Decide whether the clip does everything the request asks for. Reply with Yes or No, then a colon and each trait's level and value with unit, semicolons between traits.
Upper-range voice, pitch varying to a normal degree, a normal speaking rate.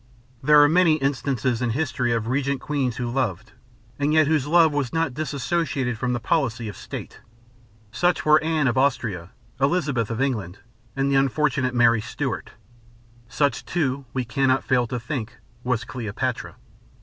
No: low, 130 Hz; average, 3.6 semitones; average, 160 wpm